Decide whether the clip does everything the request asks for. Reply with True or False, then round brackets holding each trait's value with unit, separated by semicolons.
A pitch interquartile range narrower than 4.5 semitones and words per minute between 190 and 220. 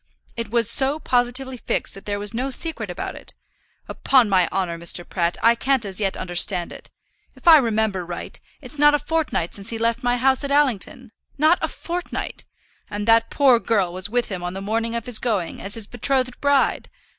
False (5.2 semitones; 200 wpm)